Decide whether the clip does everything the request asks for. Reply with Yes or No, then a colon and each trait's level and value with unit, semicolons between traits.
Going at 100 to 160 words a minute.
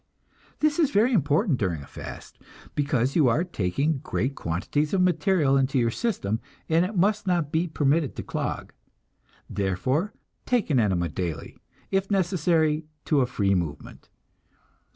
Yes: average, 150 wpm